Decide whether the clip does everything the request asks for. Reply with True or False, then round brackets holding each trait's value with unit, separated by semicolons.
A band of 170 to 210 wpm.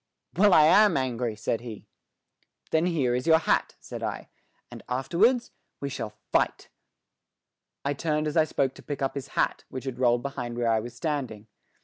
True (180 wpm)